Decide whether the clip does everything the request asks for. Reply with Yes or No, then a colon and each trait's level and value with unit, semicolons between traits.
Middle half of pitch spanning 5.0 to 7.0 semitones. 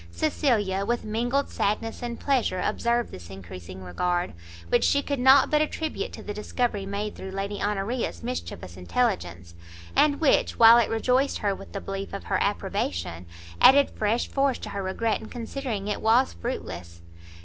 Yes: average, 5.3 semitones